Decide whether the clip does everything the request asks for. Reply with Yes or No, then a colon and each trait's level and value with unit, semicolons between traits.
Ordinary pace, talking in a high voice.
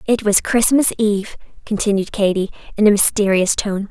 Yes: average, 155 wpm; high, 210 Hz